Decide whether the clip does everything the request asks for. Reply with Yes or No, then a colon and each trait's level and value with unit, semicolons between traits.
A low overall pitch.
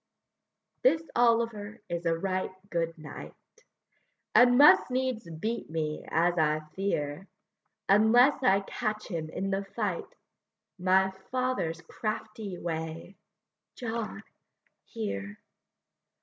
No: high, 195 Hz